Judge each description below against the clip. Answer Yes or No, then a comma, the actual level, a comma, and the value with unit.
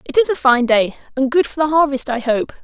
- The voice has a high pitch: Yes, very high, 275 Hz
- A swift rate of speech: Yes, fast, 275 wpm